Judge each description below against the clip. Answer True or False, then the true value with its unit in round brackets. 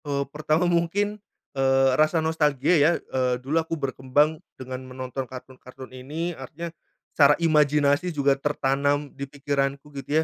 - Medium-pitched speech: True (145 Hz)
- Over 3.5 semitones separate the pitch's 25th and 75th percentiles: False (2.7 semitones)